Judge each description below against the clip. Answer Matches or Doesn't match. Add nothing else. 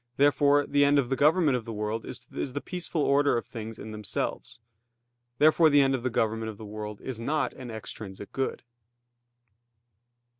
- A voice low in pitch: Matches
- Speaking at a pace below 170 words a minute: Doesn't match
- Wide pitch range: Doesn't match